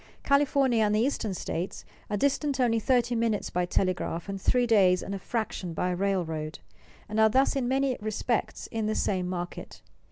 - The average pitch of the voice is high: Yes, high, 215 Hz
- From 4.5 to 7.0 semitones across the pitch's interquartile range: Yes, average, 5.1 semitones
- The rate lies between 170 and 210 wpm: Yes, average, 180 wpm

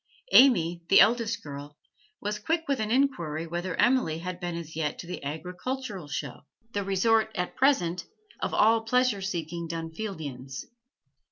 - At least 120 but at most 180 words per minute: Yes, average, 150 wpm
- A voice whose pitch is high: No, medium, 180 Hz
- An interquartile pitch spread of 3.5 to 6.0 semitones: Yes, wide, 5.6 semitones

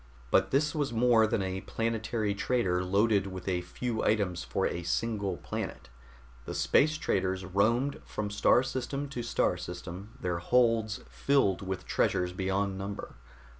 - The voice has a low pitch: Yes, low, 100 Hz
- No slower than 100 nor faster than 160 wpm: Yes, average, 150 wpm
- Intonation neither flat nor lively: Yes, average, 4.0 semitones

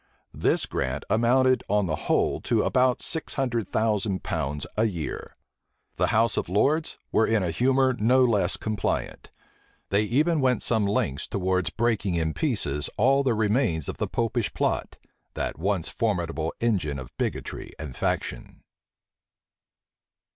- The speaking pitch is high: No, low, 105 Hz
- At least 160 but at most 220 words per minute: No, average, 145 wpm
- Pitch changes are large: Yes, wide, 6.0 semitones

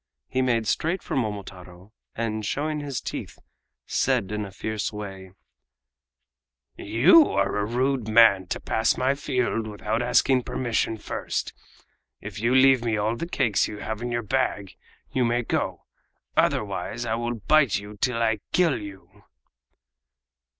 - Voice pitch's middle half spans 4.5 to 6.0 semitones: No, average, 3.6 semitones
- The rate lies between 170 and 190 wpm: No, average, 150 wpm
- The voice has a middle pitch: No, low, 115 Hz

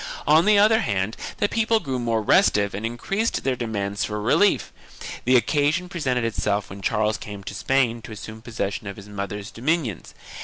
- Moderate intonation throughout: No, wide, 6.7 semitones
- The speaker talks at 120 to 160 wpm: No, average, 185 wpm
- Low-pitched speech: Yes, low, 115 Hz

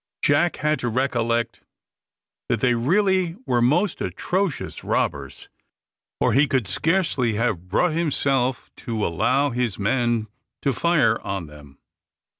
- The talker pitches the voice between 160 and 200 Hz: No, low, 125 Hz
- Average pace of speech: No, slow, 125 wpm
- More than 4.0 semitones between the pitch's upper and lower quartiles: Yes, average, 5.2 semitones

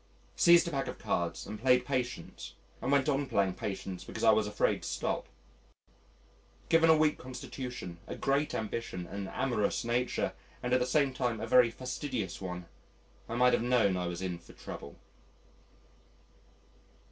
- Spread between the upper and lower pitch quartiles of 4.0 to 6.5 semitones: Yes, average, 5.1 semitones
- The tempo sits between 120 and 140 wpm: No, average, 165 wpm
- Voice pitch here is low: Yes, low, 125 Hz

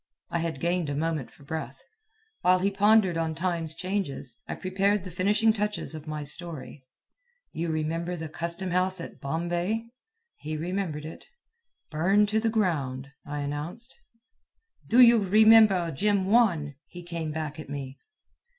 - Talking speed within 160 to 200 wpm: No, average, 150 wpm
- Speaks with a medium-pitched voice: Yes, medium, 170 Hz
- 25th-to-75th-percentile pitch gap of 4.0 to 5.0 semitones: Yes, average, 4.3 semitones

